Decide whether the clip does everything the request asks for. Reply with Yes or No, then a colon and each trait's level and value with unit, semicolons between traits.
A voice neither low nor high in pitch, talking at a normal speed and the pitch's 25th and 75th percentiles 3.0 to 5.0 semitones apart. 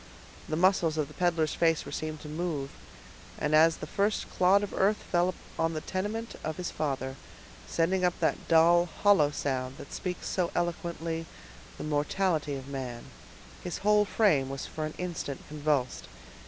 Yes: medium, 165 Hz; average, 165 wpm; average, 3.4 semitones